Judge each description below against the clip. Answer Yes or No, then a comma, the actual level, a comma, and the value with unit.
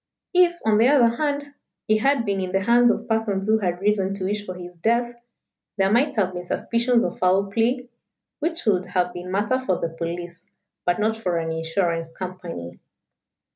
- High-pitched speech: Yes, high, 200 Hz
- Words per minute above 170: Yes, average, 190 wpm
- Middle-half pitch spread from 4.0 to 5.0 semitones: Yes, average, 4.7 semitones